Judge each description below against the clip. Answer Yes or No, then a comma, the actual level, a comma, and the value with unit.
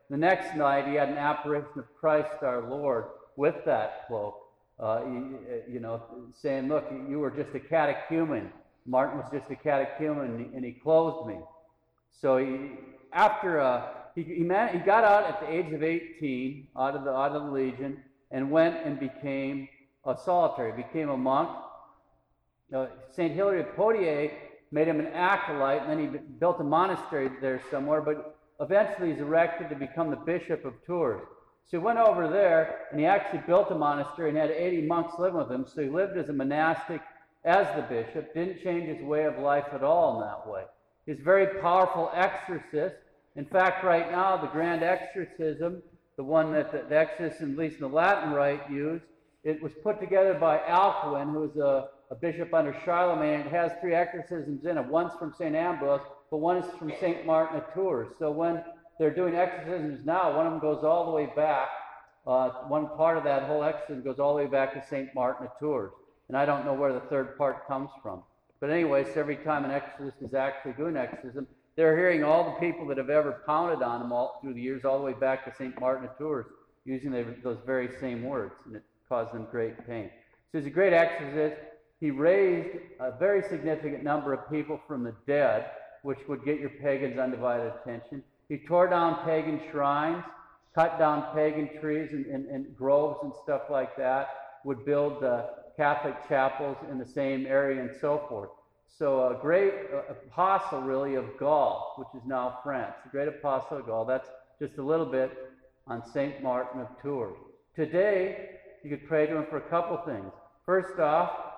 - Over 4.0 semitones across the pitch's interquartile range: No, average, 3.6 semitones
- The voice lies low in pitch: No, medium, 150 Hz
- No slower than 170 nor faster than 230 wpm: Yes, average, 195 wpm